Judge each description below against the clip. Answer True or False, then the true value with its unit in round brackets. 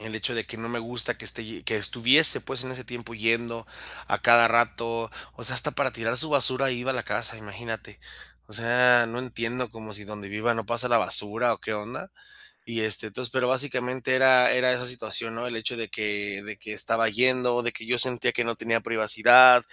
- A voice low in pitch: True (115 Hz)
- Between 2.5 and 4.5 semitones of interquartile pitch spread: False (2.0 semitones)